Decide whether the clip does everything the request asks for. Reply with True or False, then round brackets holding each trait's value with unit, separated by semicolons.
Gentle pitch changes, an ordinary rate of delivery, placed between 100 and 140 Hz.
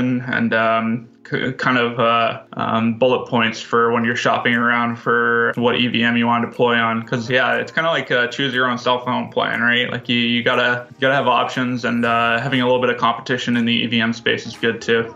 False (1.1 semitones; 230 wpm; 120 Hz)